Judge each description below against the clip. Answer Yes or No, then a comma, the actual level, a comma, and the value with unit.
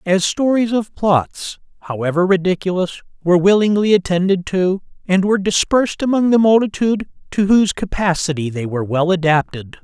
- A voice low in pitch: No, medium, 185 Hz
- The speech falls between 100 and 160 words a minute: Yes, average, 140 wpm